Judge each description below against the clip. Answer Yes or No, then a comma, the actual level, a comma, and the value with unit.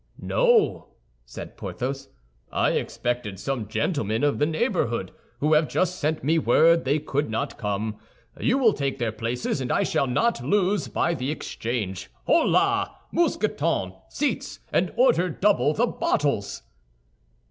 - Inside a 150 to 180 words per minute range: No, average, 140 wpm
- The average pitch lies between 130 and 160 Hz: Yes, medium, 140 Hz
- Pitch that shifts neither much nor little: No, wide, 7.7 semitones